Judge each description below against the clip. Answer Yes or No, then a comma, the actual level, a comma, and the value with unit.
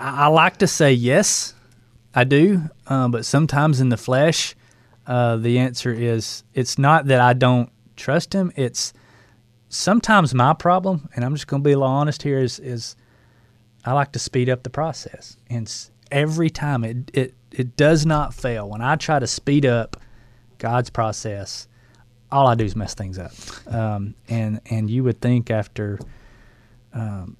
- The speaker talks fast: No, average, 175 wpm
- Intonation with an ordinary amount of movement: Yes, average, 3.5 semitones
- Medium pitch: No, low, 125 Hz